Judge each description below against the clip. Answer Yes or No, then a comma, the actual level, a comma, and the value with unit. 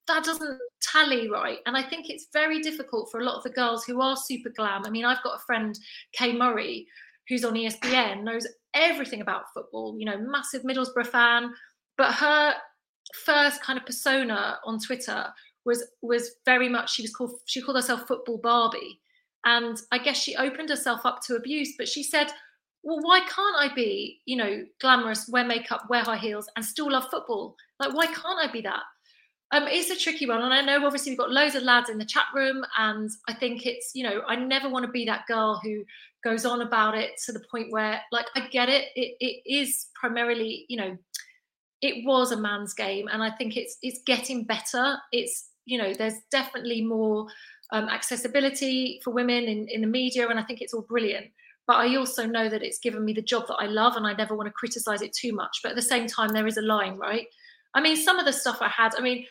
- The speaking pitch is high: Yes, high, 245 Hz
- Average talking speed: No, fast, 220 wpm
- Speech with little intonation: No, average, 3.1 semitones